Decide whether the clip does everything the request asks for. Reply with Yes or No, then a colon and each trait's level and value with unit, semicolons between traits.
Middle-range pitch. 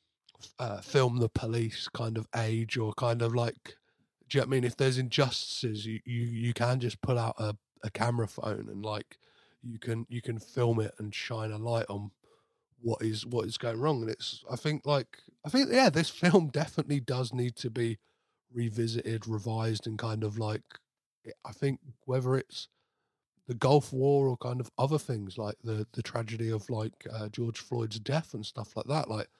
No: low, 115 Hz